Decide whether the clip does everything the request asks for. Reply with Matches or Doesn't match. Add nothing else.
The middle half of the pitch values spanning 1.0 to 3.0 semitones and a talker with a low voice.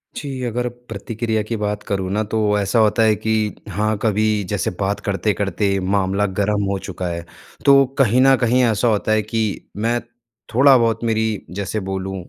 Matches